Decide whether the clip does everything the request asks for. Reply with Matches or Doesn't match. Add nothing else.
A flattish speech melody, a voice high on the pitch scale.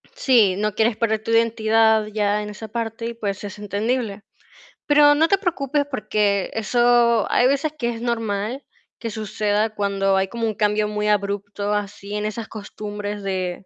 Matches